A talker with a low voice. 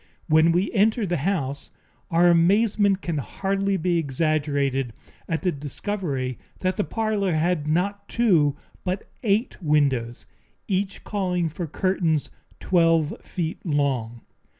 No: medium, 170 Hz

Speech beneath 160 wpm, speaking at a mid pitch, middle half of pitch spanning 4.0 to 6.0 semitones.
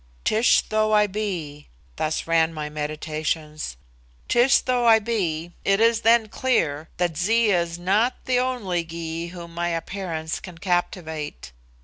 Yes: average, 140 wpm; medium, 175 Hz; average, 5.1 semitones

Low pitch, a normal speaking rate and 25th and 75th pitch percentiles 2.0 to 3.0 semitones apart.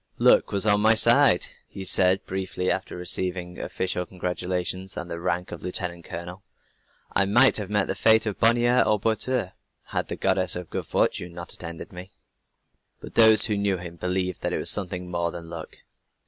Yes: very low, 95 Hz; average, 185 wpm; average, 2.7 semitones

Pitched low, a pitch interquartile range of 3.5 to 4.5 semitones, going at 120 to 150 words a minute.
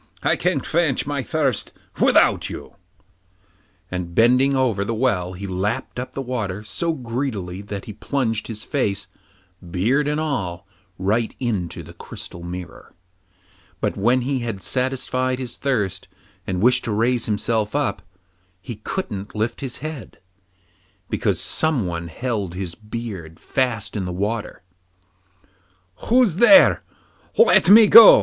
No: low, 115 Hz; average, 5.2 semitones; slow, 135 wpm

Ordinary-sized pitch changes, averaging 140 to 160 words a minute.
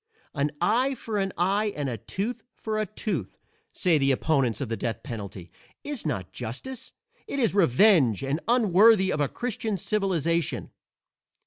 No: wide, 8.2 semitones; average, 155 wpm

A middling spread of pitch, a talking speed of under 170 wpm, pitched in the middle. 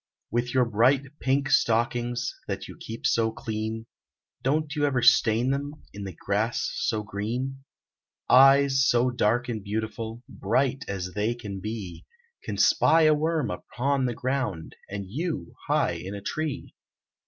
No: average, 4.0 semitones; average, 150 wpm; low, 120 Hz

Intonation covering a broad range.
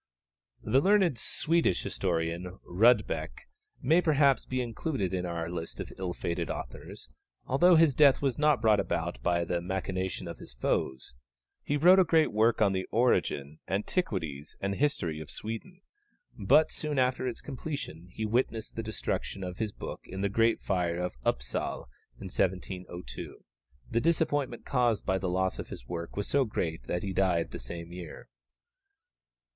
Yes: wide, 7.1 semitones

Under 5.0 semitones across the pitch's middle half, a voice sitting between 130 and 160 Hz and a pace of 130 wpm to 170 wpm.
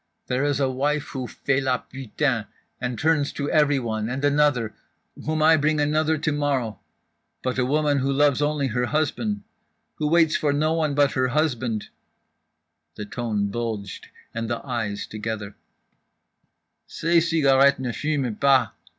Yes: average, 3.7 semitones; medium, 140 Hz; average, 150 wpm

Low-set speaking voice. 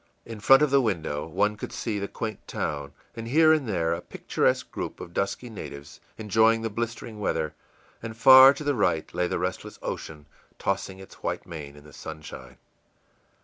Yes: low, 105 Hz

